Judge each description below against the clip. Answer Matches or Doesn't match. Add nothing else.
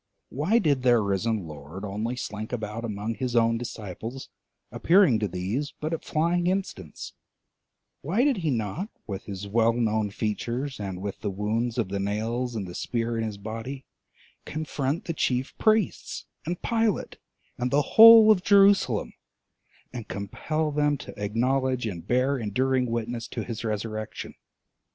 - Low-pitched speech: Matches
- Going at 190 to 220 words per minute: Doesn't match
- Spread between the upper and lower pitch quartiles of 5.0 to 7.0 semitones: Matches